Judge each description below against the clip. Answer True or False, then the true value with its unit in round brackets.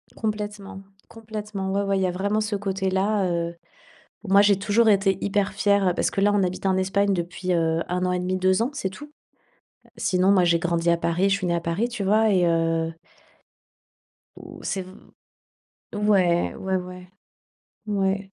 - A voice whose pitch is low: False (190 Hz)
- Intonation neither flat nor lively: False (2.1 semitones)